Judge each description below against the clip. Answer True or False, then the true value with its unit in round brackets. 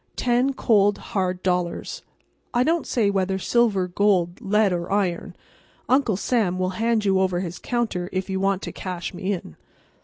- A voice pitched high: True (195 Hz)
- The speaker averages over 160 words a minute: False (155 wpm)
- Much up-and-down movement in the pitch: False (3.6 semitones)